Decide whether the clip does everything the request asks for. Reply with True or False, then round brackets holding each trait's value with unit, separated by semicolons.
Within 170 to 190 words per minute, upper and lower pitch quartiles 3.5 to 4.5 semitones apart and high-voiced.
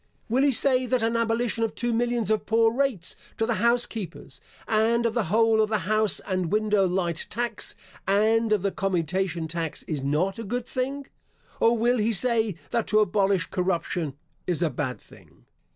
True (185 wpm; 4.0 semitones; 215 Hz)